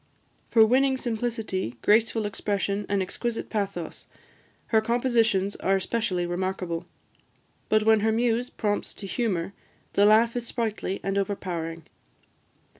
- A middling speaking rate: No, slow, 120 wpm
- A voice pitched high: Yes, high, 210 Hz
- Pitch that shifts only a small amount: No, average, 3.1 semitones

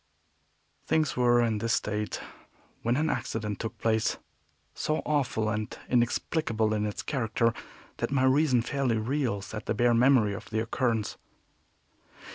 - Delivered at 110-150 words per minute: Yes, average, 140 wpm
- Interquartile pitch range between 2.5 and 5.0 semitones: Yes, average, 3.2 semitones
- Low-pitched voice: Yes, low, 115 Hz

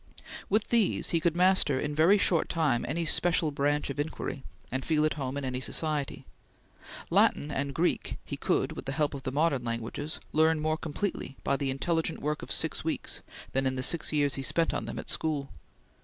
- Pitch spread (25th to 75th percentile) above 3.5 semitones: No, average, 3.0 semitones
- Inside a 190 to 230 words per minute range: Yes, average, 200 wpm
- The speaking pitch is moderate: Yes, medium, 150 Hz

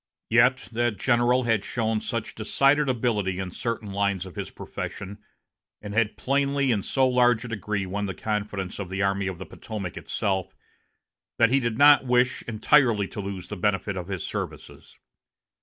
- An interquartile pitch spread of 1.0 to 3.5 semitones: No, average, 3.9 semitones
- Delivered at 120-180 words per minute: Yes, average, 175 wpm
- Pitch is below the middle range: Yes, low, 110 Hz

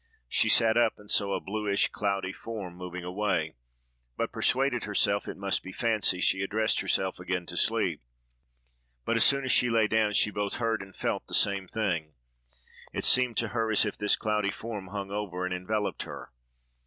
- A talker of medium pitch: No, low, 105 Hz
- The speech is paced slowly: No, average, 190 wpm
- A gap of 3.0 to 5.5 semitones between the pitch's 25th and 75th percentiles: No, narrow, 2.6 semitones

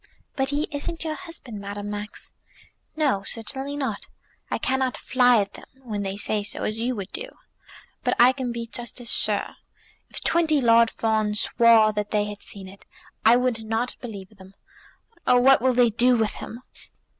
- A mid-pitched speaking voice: No, high, 235 Hz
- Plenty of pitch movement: No, average, 3.7 semitones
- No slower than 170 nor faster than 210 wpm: Yes, average, 185 wpm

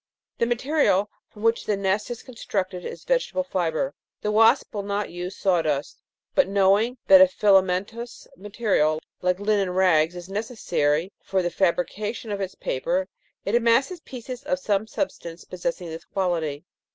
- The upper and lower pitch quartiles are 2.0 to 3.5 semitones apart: No, average, 4.4 semitones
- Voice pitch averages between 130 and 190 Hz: No, high, 200 Hz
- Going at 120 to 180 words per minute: Yes, average, 160 wpm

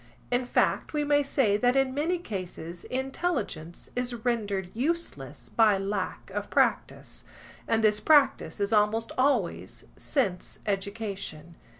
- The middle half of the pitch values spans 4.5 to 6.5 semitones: Yes, average, 5.3 semitones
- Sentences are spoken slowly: Yes, slow, 125 wpm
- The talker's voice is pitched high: Yes, high, 225 Hz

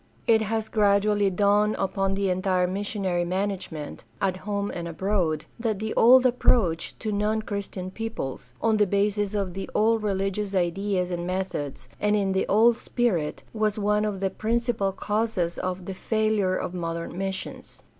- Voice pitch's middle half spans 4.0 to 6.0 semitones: No, narrow, 2.4 semitones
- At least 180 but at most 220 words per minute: No, average, 160 wpm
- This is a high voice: Yes, high, 200 Hz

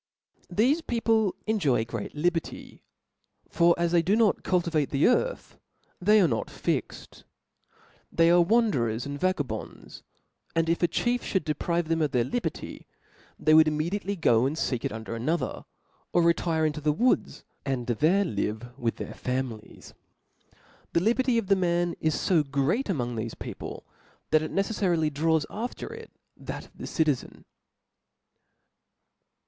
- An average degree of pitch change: No, wide, 5.9 semitones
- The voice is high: No, medium, 165 Hz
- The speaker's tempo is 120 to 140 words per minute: No, average, 155 wpm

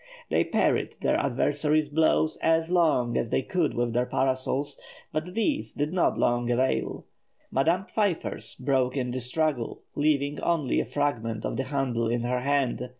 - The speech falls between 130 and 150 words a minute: No, average, 160 wpm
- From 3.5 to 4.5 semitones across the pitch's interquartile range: Yes, average, 4.0 semitones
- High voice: No, medium, 140 Hz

